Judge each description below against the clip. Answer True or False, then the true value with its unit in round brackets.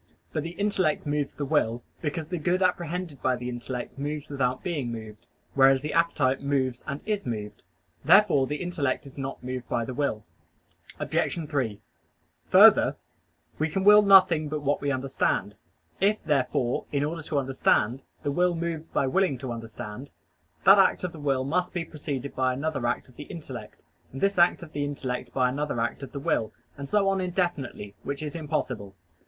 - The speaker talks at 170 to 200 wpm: True (185 wpm)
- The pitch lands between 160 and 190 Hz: False (145 Hz)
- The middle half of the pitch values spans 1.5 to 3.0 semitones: False (4.6 semitones)